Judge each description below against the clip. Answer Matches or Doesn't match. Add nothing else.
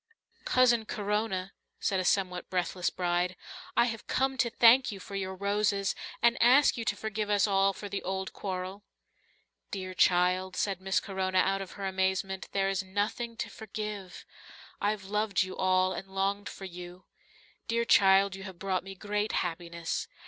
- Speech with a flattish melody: Matches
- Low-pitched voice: Doesn't match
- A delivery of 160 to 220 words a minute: Matches